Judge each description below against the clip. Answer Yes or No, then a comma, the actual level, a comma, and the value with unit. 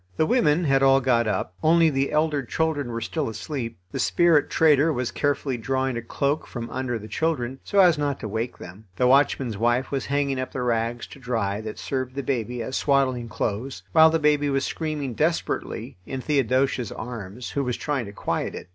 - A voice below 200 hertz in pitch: Yes, low, 135 Hz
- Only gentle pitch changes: No, average, 3.7 semitones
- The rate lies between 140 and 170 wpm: No, average, 200 wpm